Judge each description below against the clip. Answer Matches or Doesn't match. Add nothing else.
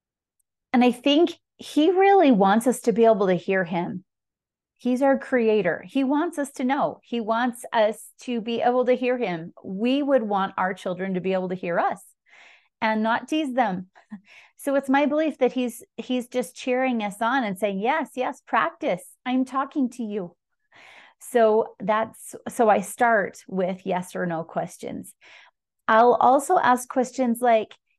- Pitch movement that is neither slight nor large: Matches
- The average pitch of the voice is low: Doesn't match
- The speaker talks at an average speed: Matches